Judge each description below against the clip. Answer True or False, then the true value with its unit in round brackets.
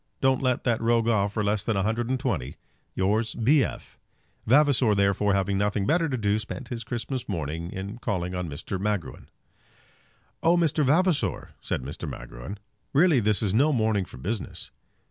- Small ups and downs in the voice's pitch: False (4.6 semitones)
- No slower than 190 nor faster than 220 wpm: False (170 wpm)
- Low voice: True (110 Hz)